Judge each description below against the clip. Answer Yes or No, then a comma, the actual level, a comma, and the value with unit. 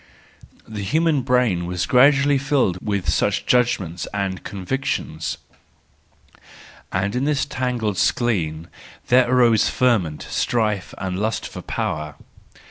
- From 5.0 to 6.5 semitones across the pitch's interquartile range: Yes, average, 5.3 semitones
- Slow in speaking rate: Yes, slow, 115 wpm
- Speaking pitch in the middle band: No, low, 110 Hz